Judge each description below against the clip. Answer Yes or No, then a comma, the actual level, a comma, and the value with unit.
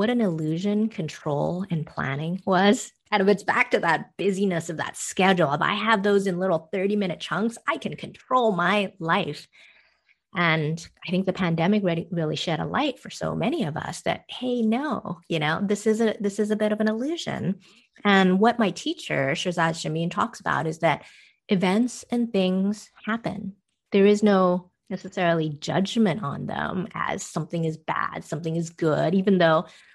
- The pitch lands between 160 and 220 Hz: Yes, high, 190 Hz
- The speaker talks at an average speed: Yes, average, 180 wpm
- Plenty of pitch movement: No, average, 4.0 semitones